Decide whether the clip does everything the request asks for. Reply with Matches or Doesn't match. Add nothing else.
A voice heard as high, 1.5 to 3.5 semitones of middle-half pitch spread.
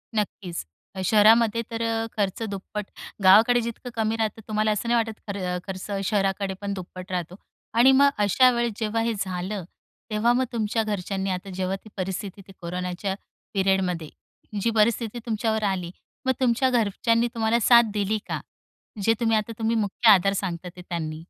Matches